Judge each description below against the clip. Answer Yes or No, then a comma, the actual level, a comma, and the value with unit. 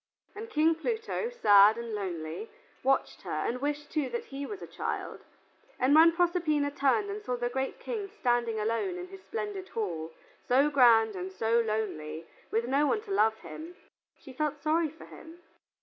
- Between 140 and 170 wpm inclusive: No, average, 180 wpm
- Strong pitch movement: Yes, wide, 7.8 semitones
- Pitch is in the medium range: No, very high, 285 Hz